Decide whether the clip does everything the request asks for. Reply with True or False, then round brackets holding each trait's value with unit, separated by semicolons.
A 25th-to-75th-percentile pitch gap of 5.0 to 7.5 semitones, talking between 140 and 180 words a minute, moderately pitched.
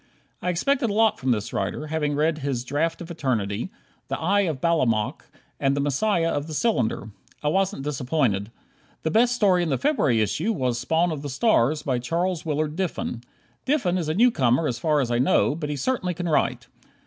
False (5.4 semitones; 195 wpm; 155 Hz)